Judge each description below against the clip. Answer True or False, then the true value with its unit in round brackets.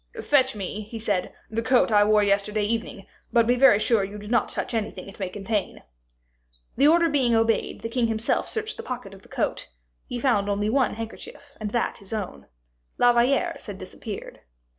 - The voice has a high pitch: True (225 Hz)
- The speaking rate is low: False (195 wpm)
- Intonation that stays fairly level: False (3.2 semitones)